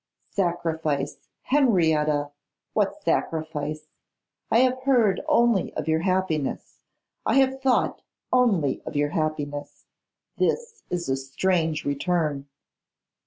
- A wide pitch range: Yes, wide, 7.7 semitones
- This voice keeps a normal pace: No, slow, 105 wpm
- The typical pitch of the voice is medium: Yes, medium, 165 Hz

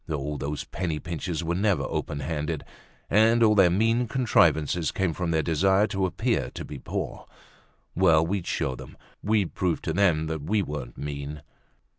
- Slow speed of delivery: No, average, 170 wpm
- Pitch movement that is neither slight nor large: Yes, average, 4.5 semitones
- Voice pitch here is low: Yes, very low, 85 Hz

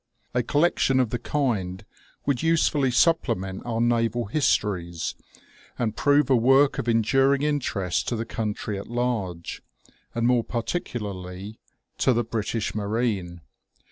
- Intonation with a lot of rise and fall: No, average, 4.2 semitones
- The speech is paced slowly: Yes, slow, 130 wpm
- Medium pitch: No, low, 115 Hz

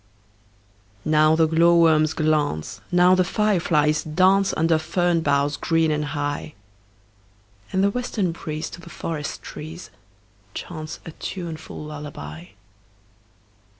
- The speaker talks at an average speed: No, slow, 115 wpm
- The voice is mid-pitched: Yes, medium, 160 Hz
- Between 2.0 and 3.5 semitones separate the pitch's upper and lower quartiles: Yes, narrow, 2.4 semitones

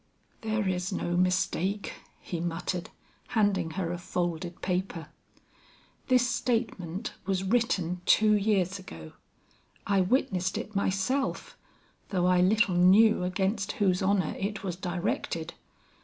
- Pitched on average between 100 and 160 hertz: No, high, 190 Hz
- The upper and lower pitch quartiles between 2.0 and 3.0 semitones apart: Yes, narrow, 2.5 semitones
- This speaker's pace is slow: Yes, slow, 120 wpm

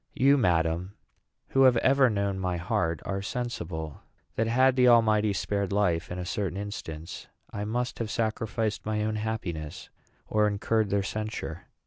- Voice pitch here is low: Yes, low, 105 Hz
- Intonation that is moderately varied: Yes, average, 3.9 semitones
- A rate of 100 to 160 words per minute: Yes, average, 155 wpm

